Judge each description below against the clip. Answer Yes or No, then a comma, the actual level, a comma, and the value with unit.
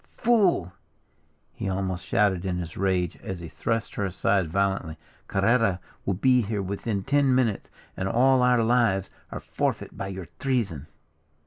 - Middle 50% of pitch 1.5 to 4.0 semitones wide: No, average, 4.5 semitones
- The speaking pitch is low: Yes, low, 100 Hz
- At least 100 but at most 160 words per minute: Yes, average, 150 wpm